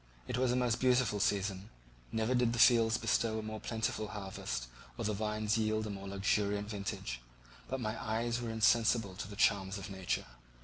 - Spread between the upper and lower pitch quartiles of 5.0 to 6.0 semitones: No, narrow, 2.4 semitones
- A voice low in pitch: Yes, low, 110 Hz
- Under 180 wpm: No, average, 185 wpm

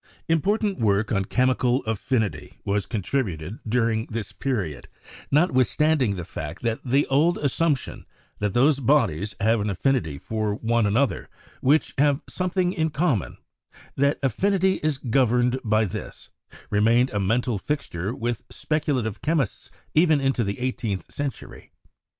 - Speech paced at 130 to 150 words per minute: Yes, average, 140 wpm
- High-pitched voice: No, low, 125 Hz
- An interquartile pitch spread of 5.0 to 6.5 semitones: Yes, average, 5.3 semitones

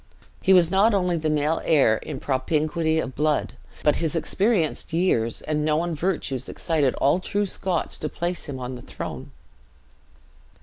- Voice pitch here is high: No, medium, 155 Hz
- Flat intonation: No, average, 3.3 semitones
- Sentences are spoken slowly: No, average, 160 wpm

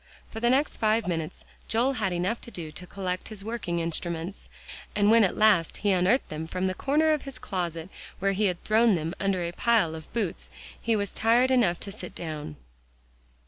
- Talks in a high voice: Yes, high, 195 Hz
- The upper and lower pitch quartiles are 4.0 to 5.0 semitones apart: Yes, average, 4.7 semitones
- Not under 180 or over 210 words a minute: Yes, average, 200 wpm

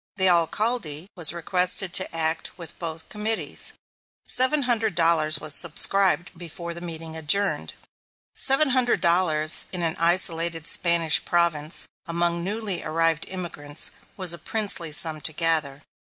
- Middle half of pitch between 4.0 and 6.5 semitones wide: No, average, 2.8 semitones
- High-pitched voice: No, medium, 170 Hz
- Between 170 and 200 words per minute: No, slow, 135 wpm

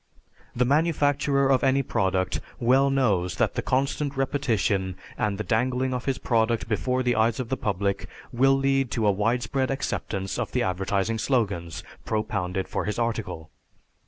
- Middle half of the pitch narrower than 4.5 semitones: No, average, 4.9 semitones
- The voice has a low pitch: Yes, low, 115 Hz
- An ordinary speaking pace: Yes, average, 155 wpm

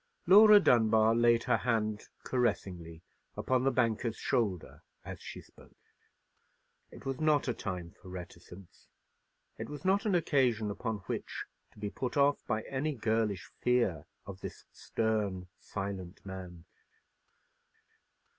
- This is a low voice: Yes, low, 110 Hz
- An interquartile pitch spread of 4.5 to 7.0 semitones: Yes, average, 5.0 semitones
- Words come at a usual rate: No, slow, 130 wpm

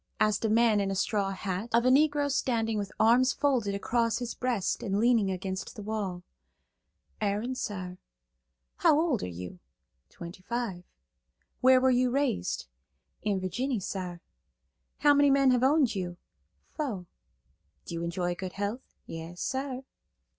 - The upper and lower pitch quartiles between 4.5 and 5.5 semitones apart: Yes, average, 5.2 semitones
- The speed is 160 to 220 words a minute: No, average, 150 wpm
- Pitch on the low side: No, high, 215 Hz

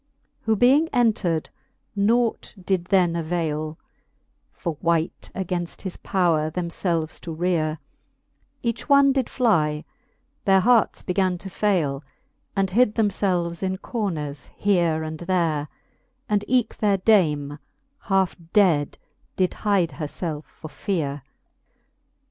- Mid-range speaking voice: Yes, medium, 180 Hz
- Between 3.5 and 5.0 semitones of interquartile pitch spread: Yes, average, 4.5 semitones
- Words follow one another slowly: Yes, slow, 125 wpm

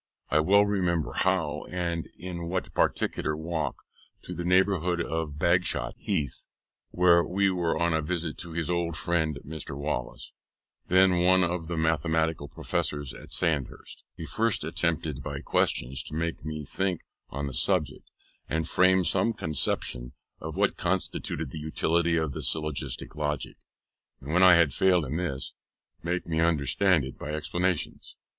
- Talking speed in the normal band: Yes, average, 155 wpm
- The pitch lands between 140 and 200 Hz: No, very low, 80 Hz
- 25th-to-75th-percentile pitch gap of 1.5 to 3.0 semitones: Yes, average, 2.7 semitones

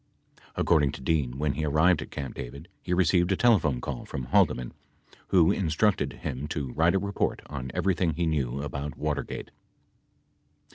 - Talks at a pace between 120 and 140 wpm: No, average, 160 wpm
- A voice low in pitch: Yes, very low, 75 Hz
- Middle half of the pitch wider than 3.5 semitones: Yes, average, 4.1 semitones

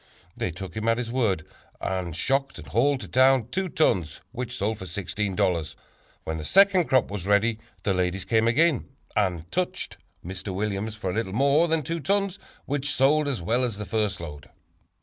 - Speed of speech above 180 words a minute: Yes, average, 190 wpm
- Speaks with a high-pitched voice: No, low, 110 Hz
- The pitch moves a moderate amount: No, wide, 6.3 semitones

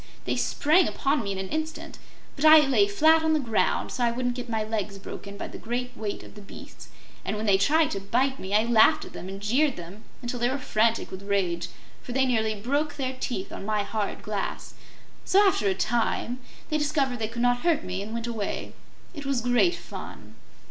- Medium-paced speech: No, fast, 220 wpm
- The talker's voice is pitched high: Yes, high, 235 Hz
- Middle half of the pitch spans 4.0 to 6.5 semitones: Yes, average, 5.0 semitones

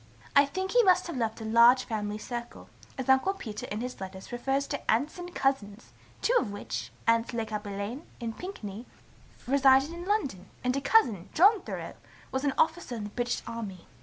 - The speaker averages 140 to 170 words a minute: No, average, 190 wpm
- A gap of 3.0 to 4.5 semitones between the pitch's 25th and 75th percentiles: No, average, 4.9 semitones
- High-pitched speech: Yes, high, 245 Hz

